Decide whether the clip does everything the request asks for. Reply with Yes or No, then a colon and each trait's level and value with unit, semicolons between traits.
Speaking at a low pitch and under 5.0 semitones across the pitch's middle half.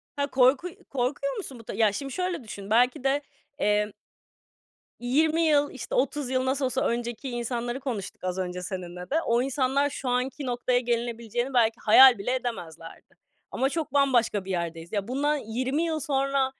No: very high, 250 Hz; average, 3.6 semitones